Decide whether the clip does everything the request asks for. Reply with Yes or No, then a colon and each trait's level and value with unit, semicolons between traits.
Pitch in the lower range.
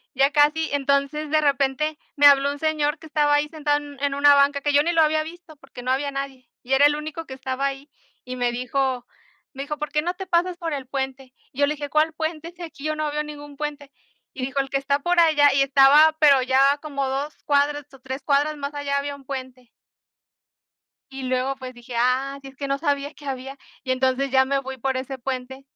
No: very high, 280 Hz